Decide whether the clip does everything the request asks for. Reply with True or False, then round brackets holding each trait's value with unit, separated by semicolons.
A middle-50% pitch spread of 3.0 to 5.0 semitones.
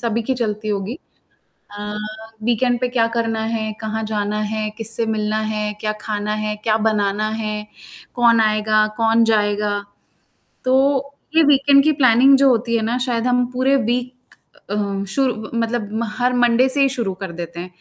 False (2.5 semitones)